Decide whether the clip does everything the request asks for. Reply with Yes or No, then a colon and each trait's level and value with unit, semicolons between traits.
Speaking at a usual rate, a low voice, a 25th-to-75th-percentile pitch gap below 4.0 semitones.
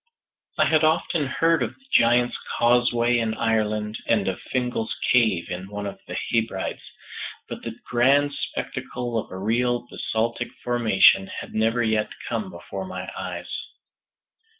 Yes: average, 145 wpm; low, 115 Hz; average, 3.1 semitones